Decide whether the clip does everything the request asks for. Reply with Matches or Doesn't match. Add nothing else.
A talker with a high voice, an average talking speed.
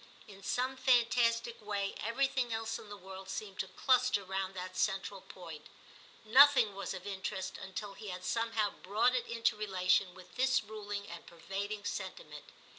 Matches